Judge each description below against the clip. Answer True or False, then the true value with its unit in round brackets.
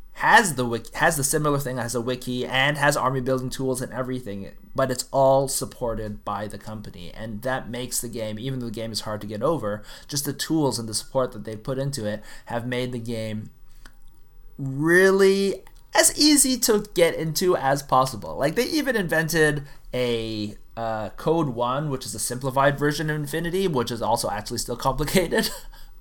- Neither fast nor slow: True (190 wpm)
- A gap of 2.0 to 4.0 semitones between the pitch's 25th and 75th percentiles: False (4.6 semitones)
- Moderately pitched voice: False (130 Hz)